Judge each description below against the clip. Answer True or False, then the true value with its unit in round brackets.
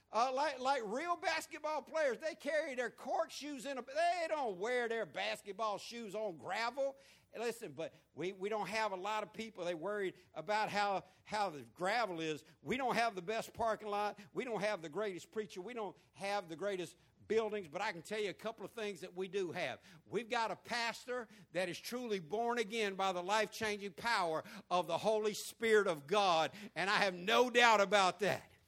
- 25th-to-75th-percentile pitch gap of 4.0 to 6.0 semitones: False (3.6 semitones)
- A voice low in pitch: False (215 Hz)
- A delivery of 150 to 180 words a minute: False (205 wpm)